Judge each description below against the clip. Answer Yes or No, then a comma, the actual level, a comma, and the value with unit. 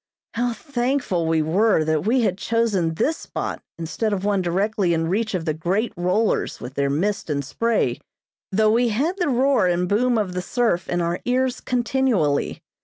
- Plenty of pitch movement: Yes, wide, 5.7 semitones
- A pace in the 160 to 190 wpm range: Yes, average, 180 wpm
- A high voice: Yes, high, 205 Hz